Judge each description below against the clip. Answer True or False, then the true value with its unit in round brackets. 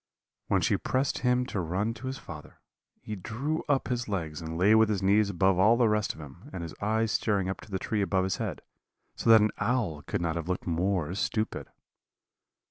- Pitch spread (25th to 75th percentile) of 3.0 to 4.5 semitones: True (4.1 semitones)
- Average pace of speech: False (215 wpm)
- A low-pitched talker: True (100 Hz)